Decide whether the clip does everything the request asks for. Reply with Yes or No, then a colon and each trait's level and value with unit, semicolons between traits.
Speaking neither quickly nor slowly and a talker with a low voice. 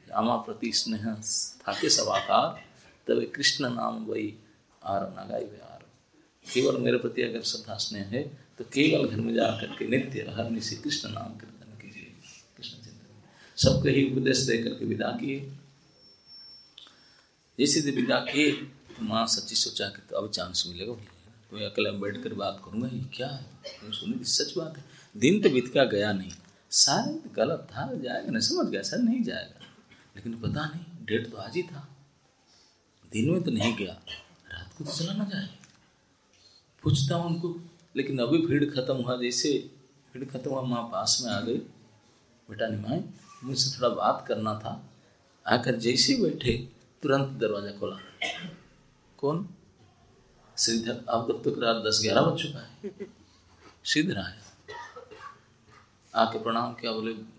Yes: average, 155 wpm; low, 125 Hz